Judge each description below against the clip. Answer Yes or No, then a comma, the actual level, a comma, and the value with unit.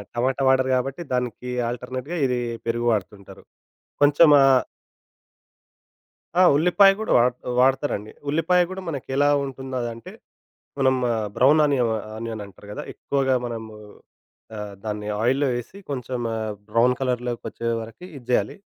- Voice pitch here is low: Yes, low, 125 Hz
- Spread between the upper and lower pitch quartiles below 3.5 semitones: Yes, average, 2.9 semitones